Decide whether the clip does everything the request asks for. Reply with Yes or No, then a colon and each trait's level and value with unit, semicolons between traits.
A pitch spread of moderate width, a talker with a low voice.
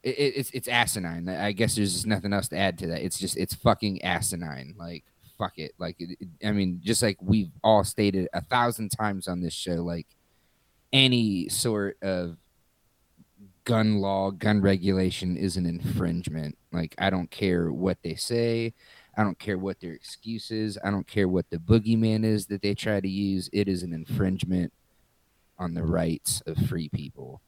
Yes: average, 3.3 semitones; very low, 95 Hz